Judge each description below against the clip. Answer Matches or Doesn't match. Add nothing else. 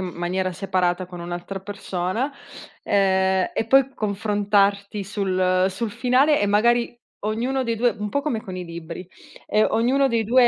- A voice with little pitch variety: Doesn't match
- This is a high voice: Matches